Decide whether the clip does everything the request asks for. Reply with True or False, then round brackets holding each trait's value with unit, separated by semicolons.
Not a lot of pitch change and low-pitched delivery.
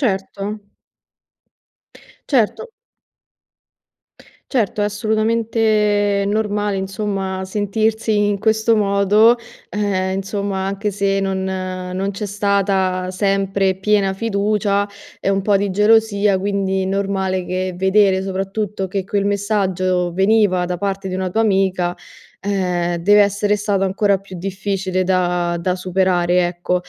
False (1.6 semitones; 195 Hz)